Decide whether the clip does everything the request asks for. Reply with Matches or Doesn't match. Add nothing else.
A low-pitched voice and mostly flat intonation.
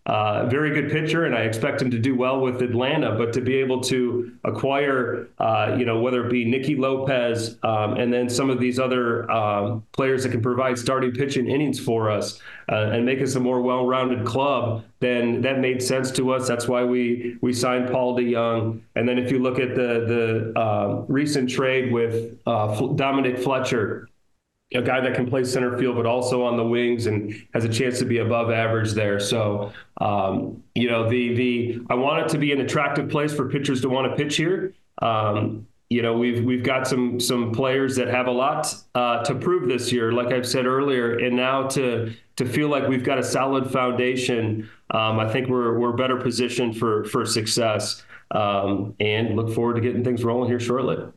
Matches